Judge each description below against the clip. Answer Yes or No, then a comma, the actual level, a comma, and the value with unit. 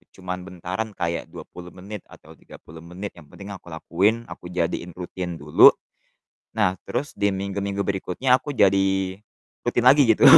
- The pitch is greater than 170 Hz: No, very low, 95 Hz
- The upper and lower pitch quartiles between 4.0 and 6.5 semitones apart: No, narrow, 2.4 semitones